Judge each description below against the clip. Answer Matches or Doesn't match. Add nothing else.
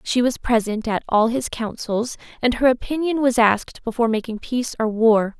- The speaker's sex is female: Matches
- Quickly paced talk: Doesn't match